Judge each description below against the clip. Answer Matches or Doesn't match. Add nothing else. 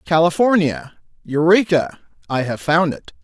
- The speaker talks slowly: Matches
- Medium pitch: Matches